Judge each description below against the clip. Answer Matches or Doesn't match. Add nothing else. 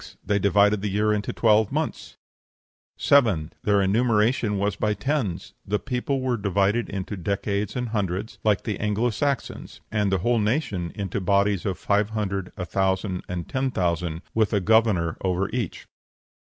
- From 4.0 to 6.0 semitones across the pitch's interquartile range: Doesn't match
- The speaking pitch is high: Doesn't match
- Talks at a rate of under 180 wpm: Matches